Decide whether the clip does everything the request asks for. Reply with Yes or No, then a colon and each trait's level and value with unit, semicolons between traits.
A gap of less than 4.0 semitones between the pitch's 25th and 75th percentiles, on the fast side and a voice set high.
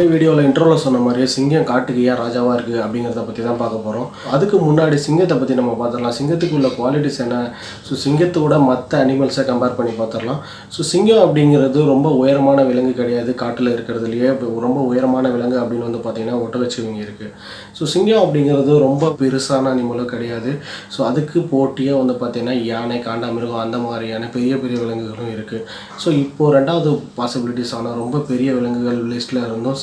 No: average, 2.8 semitones; fast, 165 wpm; low, 125 Hz